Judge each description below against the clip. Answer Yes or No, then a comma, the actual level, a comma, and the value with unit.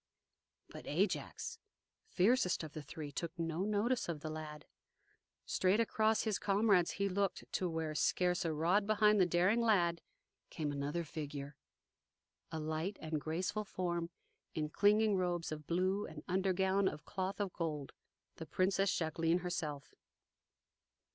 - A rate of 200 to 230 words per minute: No, average, 140 wpm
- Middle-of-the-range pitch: Yes, medium, 180 Hz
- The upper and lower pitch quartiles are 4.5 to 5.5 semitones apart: No, average, 4.0 semitones